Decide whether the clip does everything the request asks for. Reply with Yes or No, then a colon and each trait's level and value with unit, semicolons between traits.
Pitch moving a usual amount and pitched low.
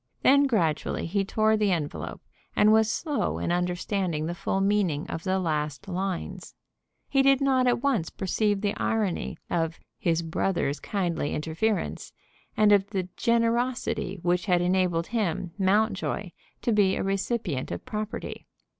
No: average, 4.0 semitones; high, 195 Hz